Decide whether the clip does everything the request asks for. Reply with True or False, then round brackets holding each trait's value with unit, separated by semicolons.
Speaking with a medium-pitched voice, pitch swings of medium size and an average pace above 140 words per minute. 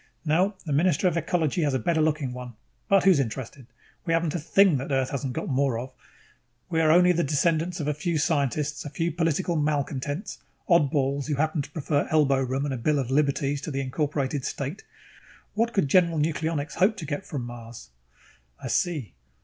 True (150 Hz; 3.3 semitones; 190 wpm)